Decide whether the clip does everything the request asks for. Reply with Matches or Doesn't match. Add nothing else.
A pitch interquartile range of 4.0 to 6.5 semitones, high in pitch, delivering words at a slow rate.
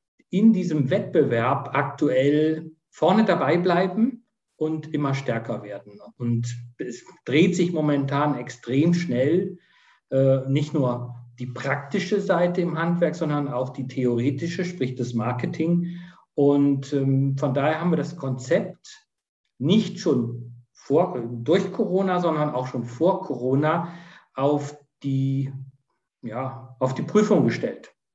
Doesn't match